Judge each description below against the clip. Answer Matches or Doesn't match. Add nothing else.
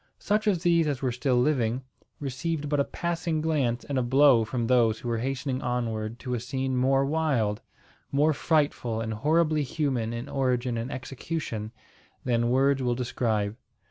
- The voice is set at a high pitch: Doesn't match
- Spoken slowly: Doesn't match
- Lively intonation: Doesn't match